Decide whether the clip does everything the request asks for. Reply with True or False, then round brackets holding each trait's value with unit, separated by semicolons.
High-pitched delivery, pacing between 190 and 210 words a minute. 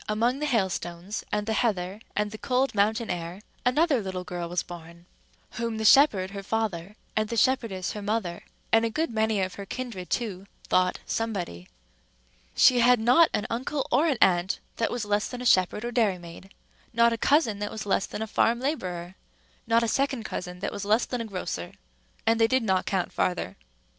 True (215 Hz; 195 wpm)